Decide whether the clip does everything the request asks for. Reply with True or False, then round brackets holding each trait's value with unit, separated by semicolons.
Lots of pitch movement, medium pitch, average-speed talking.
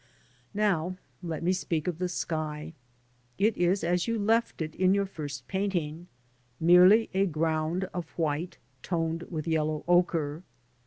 False (2.9 semitones; 170 Hz; 150 wpm)